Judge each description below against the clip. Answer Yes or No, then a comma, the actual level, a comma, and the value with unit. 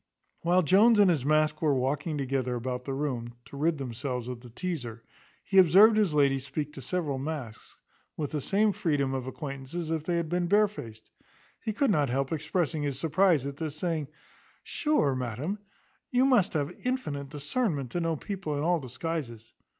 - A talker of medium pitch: Yes, medium, 150 Hz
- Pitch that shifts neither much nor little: Yes, average, 4.7 semitones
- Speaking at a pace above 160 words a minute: Yes, average, 180 wpm